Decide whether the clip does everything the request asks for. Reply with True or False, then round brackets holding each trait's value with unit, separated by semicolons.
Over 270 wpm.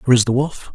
True (320 wpm)